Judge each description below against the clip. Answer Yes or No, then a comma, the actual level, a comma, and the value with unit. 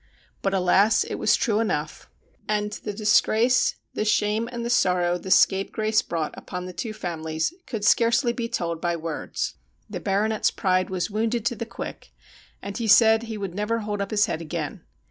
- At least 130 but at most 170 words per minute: No, average, 185 wpm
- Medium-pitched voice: No, high, 210 Hz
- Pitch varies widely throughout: No, average, 3.5 semitones